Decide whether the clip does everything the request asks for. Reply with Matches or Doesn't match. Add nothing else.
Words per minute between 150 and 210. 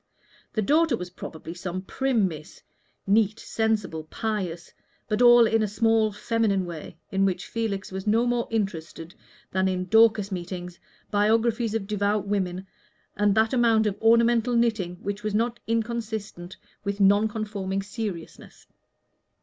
Doesn't match